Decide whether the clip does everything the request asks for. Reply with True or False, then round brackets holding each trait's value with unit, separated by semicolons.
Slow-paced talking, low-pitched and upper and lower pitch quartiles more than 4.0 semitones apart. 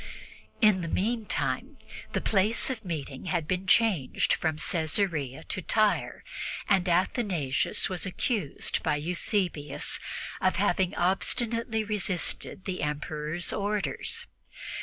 False (110 wpm; 185 Hz; 4.6 semitones)